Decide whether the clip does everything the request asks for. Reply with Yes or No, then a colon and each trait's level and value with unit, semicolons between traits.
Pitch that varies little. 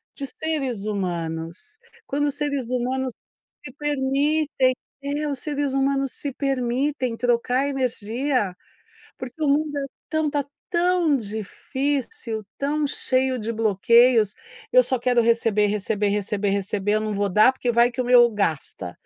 No: average, 4.7 semitones